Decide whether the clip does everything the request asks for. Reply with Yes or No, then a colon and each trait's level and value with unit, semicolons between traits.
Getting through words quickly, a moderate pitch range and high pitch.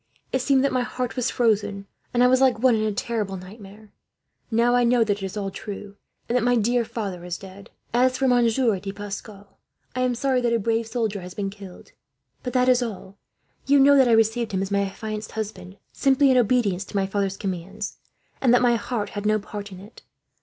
Yes: fast, 225 wpm; average, 3.6 semitones; high, 220 Hz